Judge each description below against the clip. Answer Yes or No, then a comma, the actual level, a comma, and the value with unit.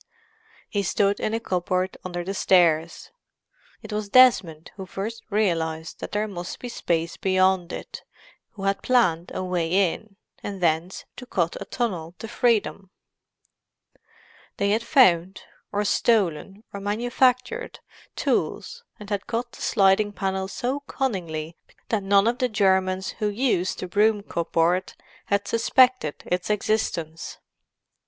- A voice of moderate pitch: No, high, 195 Hz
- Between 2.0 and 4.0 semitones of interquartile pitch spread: Yes, average, 3.7 semitones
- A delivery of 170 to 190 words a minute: No, average, 140 wpm